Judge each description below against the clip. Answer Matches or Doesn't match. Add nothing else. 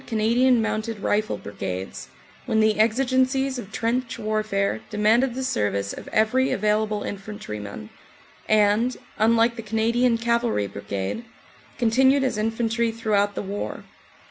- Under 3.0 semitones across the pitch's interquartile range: Matches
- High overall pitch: Matches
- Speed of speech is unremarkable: Doesn't match